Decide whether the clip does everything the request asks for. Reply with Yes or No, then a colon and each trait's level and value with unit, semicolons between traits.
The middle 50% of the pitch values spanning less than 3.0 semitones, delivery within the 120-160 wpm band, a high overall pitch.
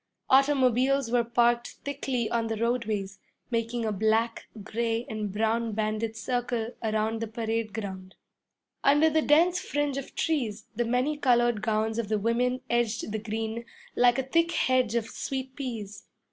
Yes: narrow, 2.6 semitones; average, 155 wpm; high, 235 Hz